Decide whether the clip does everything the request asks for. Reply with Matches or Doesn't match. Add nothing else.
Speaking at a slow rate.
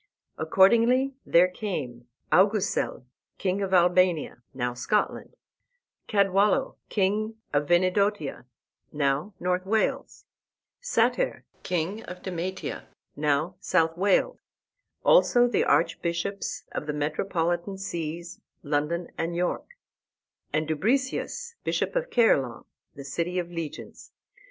Matches